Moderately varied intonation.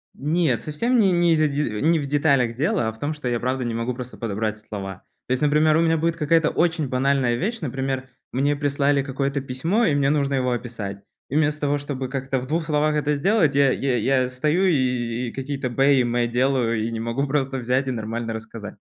Yes: average, 3.5 semitones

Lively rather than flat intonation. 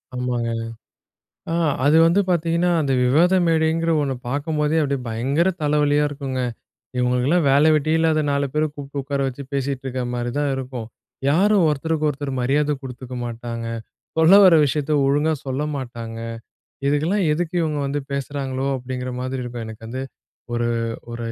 No: average, 3.3 semitones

